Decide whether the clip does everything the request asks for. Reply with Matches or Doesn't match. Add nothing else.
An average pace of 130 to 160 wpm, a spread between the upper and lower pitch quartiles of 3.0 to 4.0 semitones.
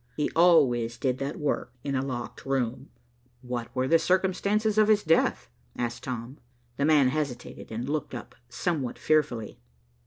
Doesn't match